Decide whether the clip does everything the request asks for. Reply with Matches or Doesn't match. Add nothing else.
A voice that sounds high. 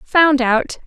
Matches